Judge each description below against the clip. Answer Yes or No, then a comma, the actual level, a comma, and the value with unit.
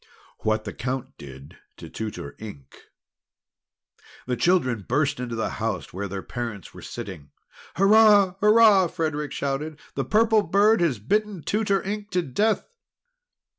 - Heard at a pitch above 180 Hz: No, medium, 150 Hz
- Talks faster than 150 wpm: No, slow, 135 wpm